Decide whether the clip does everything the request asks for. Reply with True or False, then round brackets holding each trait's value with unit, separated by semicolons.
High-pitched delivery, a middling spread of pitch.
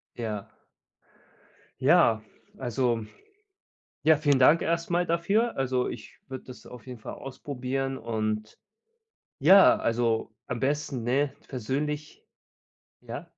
False (130 Hz; 4.1 semitones)